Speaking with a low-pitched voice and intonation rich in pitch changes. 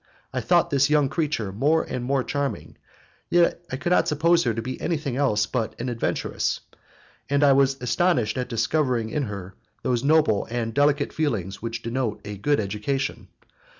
No: low, 130 Hz; average, 4.3 semitones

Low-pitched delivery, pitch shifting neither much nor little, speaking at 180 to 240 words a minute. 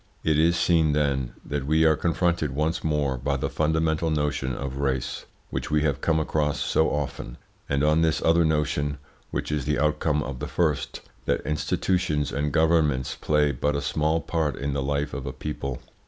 No: very low, 75 Hz; narrow, 1.9 semitones; average, 185 wpm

